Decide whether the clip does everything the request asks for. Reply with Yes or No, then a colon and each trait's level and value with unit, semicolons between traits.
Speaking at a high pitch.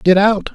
Yes: high, 200 Hz